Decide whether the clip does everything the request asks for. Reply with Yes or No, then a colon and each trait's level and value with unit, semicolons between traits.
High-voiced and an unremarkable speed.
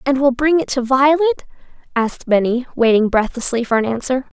Yes: very high, 255 Hz; average, 180 wpm